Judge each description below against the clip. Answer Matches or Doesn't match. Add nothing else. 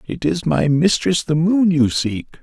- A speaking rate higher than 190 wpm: Matches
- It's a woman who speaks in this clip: Doesn't match